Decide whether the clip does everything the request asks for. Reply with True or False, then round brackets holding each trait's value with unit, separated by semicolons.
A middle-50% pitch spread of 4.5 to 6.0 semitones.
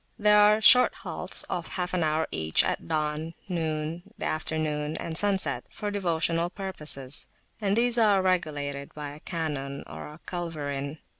False (4.1 semitones)